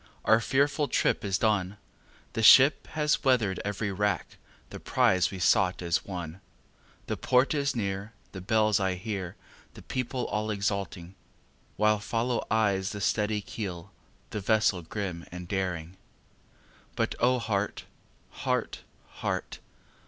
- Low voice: Yes, low, 105 Hz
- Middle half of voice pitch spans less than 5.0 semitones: Yes, average, 3.0 semitones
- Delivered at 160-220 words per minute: No, slow, 135 wpm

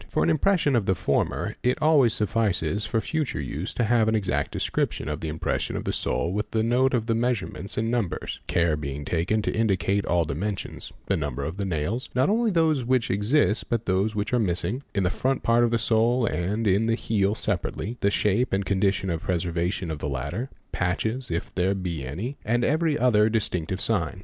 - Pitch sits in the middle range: No, low, 105 Hz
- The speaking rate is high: Yes, fast, 215 wpm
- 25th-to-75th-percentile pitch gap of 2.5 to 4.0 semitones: No, average, 4.9 semitones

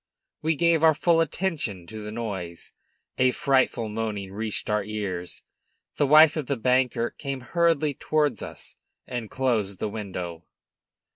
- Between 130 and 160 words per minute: Yes, average, 145 wpm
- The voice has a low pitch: Yes, low, 120 Hz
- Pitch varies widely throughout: Yes, wide, 6.0 semitones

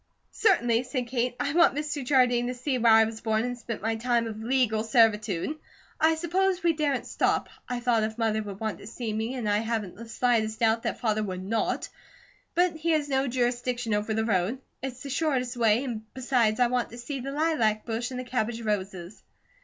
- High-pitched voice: Yes, high, 240 Hz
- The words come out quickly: Yes, fast, 210 wpm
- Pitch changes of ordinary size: Yes, average, 3.0 semitones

